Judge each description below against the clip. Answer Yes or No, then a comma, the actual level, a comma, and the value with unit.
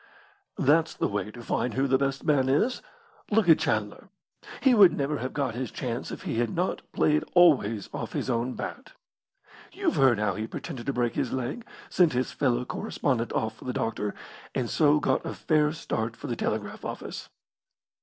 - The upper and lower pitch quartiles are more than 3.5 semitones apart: Yes, average, 4.3 semitones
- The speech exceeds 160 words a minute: Yes, average, 190 wpm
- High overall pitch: No, low, 130 Hz